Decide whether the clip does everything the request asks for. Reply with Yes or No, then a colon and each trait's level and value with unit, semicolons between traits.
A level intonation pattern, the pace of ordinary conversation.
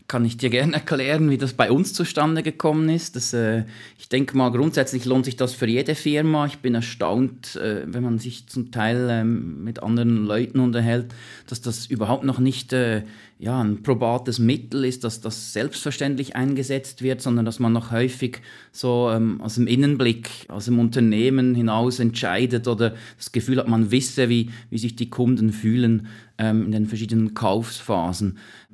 Yes: narrow, 2.3 semitones; average, 180 wpm